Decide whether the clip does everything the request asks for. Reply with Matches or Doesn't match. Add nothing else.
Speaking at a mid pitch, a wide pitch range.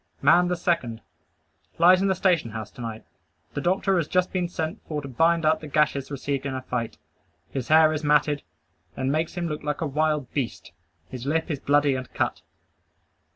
Doesn't match